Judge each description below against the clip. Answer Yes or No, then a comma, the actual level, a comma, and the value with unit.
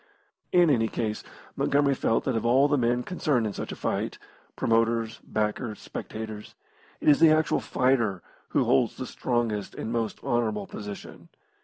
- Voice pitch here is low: Yes, low, 115 Hz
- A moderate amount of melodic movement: Yes, average, 3.5 semitones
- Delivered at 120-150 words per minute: No, average, 160 wpm